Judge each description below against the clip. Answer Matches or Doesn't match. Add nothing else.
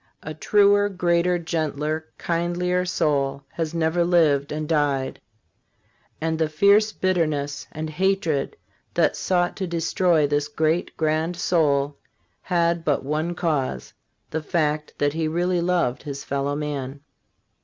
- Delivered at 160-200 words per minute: Doesn't match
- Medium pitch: Matches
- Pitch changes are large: Doesn't match